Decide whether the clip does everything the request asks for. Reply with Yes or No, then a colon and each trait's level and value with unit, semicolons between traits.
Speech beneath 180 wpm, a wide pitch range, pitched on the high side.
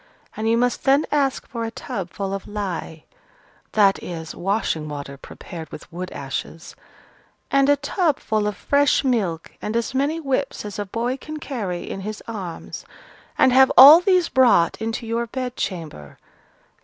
Yes: average, 165 wpm; wide, 6.7 semitones; high, 220 Hz